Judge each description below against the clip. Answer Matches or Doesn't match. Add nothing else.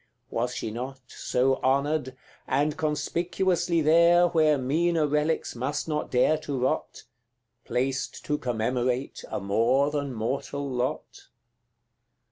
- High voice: Doesn't match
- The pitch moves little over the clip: Doesn't match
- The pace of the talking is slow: Matches